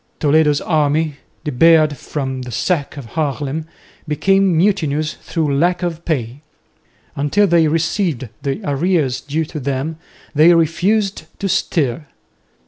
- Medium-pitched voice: Yes, medium, 155 Hz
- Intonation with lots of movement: No, average, 3.1 semitones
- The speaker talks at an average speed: No, slow, 125 wpm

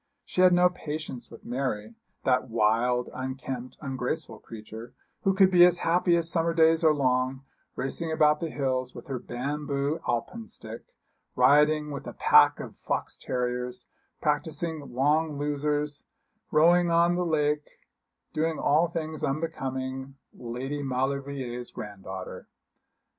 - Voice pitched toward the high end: No, medium, 140 Hz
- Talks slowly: Yes, slow, 130 wpm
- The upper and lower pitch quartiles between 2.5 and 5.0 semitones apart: Yes, average, 4.0 semitones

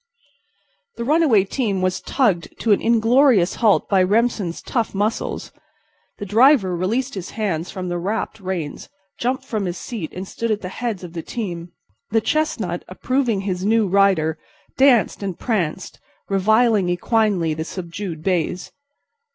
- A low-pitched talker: No, high, 200 Hz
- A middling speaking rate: Yes, average, 150 wpm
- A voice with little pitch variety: No, average, 4.2 semitones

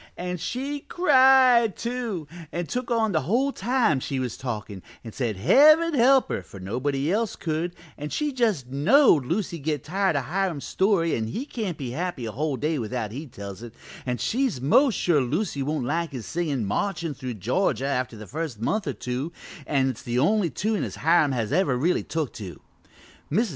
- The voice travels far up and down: Yes, wide, 9.0 semitones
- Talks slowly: No, average, 190 wpm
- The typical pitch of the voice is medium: Yes, medium, 155 Hz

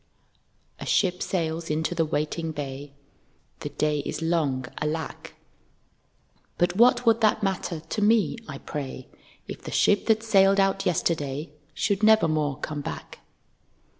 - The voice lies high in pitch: No, medium, 165 Hz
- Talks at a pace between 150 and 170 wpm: No, average, 140 wpm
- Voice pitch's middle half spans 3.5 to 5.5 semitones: Yes, average, 4.7 semitones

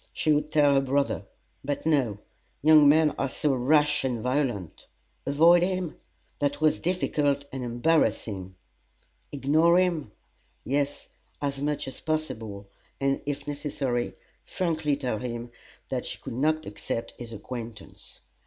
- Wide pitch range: No, average, 3.9 semitones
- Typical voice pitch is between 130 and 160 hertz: Yes, medium, 140 Hz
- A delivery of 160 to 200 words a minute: No, slow, 135 wpm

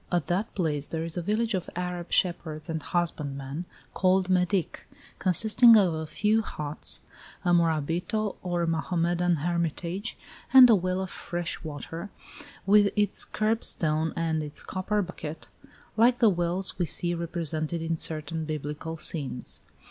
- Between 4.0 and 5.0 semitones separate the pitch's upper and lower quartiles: No, average, 2.9 semitones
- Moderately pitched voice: Yes, medium, 175 Hz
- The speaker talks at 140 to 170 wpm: Yes, average, 145 wpm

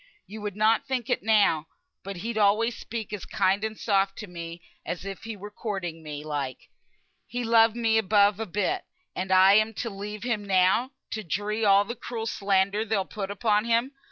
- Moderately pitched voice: No, high, 210 Hz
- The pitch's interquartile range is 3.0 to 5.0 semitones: No, narrow, 2.5 semitones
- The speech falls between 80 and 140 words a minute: No, average, 195 wpm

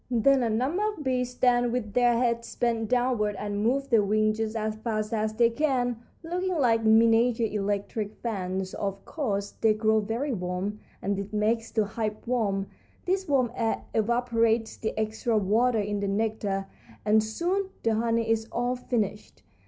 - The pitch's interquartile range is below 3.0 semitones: Yes, narrow, 2.5 semitones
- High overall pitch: Yes, high, 225 Hz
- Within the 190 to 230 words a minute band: No, average, 170 wpm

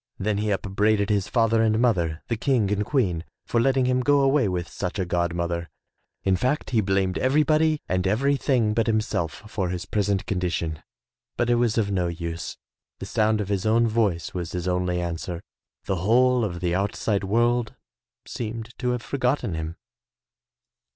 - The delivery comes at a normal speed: Yes, average, 175 wpm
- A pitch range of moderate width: Yes, average, 4.7 semitones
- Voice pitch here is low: Yes, low, 105 Hz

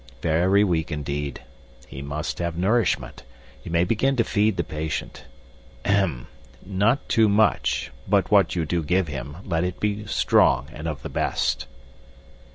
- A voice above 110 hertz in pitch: No, very low, 85 Hz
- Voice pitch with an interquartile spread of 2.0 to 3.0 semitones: No, average, 5.1 semitones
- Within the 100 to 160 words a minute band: Yes, average, 155 wpm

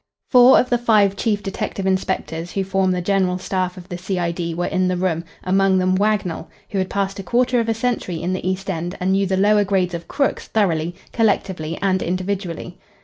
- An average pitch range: No, narrow, 2.0 semitones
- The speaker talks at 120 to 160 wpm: No, fast, 205 wpm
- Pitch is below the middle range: No, high, 190 Hz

